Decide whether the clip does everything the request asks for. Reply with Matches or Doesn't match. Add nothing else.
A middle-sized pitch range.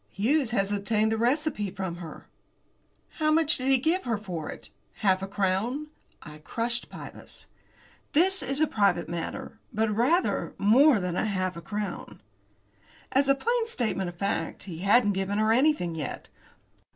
Doesn't match